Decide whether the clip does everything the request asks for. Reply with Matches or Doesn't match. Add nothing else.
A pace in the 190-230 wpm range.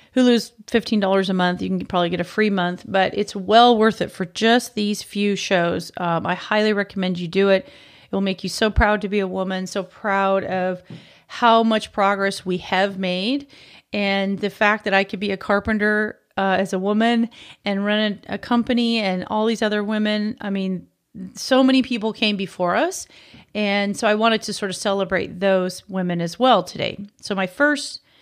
Matches